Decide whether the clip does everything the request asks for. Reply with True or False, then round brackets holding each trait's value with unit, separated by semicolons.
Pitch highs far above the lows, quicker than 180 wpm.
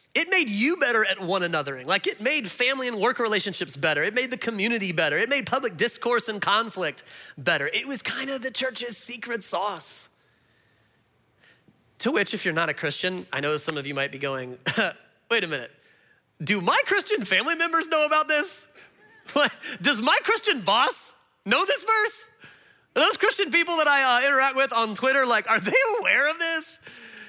True (7.6 semitones; 190 wpm)